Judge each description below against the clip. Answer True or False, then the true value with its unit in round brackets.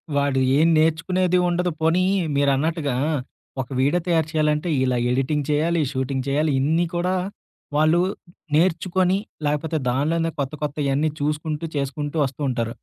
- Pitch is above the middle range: False (150 Hz)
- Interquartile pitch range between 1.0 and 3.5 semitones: True (3.0 semitones)